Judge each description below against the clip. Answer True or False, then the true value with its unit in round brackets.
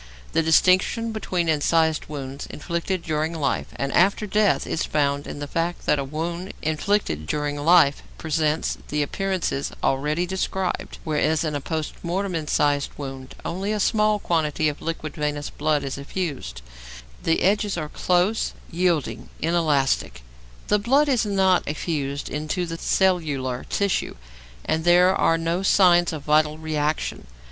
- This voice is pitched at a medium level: True (160 Hz)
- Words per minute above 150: False (145 wpm)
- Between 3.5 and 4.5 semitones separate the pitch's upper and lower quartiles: True (3.8 semitones)